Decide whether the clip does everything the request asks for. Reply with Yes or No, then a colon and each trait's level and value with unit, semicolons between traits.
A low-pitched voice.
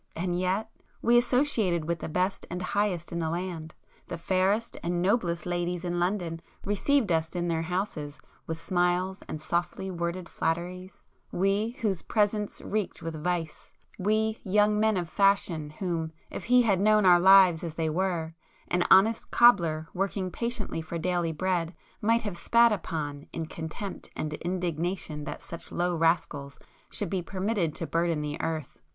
No: medium, 180 Hz